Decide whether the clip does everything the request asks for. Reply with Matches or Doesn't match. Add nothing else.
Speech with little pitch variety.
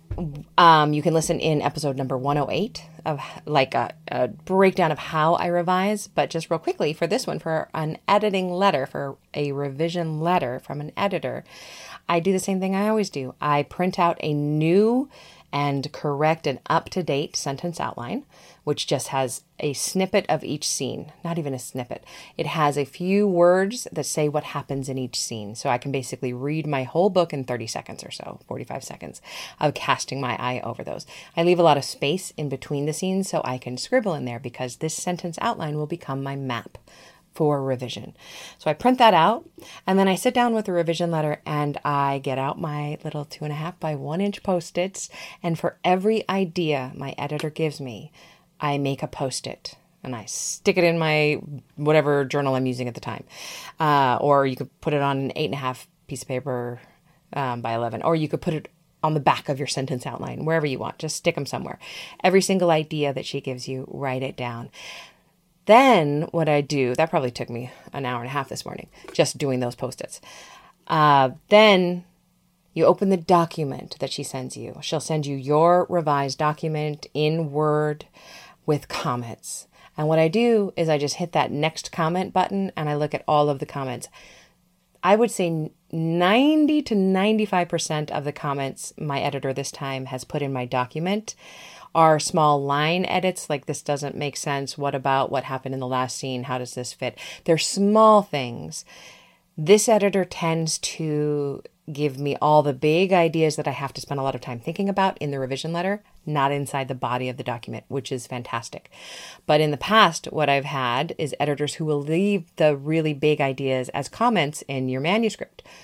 Doesn't match